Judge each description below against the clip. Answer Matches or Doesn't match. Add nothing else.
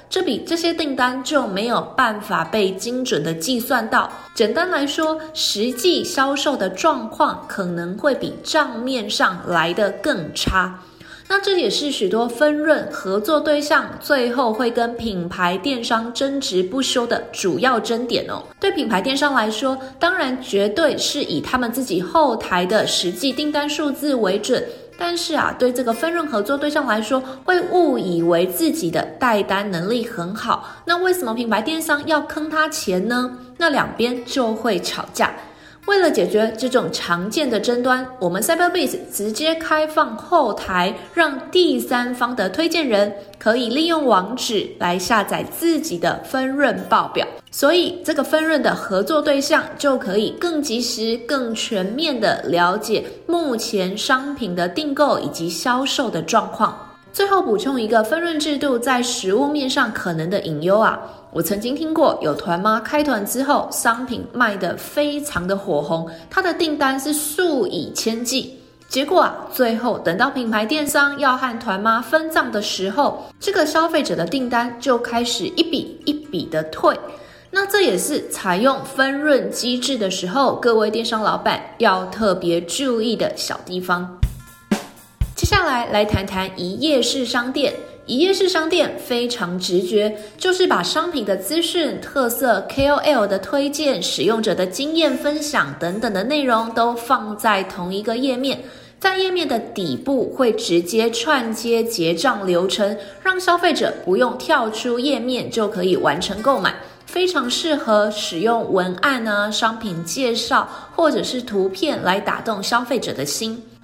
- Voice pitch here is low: Doesn't match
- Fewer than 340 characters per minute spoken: Matches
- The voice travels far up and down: Matches